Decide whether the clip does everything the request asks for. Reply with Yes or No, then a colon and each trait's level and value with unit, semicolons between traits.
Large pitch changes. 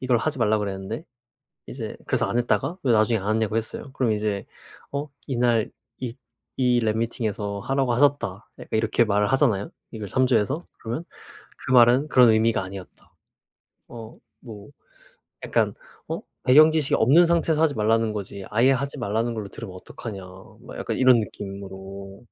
No: average, 3.8 semitones